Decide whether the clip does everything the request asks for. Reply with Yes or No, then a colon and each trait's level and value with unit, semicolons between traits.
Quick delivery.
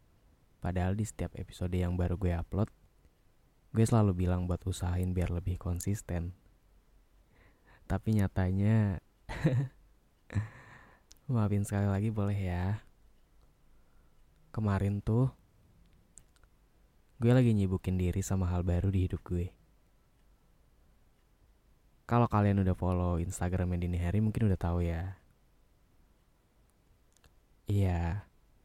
No: average, 100 wpm